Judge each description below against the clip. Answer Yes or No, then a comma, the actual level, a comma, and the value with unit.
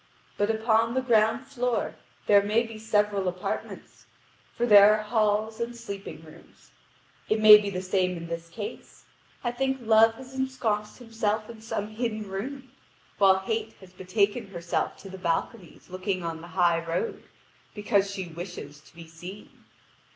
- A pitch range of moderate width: Yes, average, 3.5 semitones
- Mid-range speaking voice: No, high, 210 Hz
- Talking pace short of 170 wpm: Yes, average, 160 wpm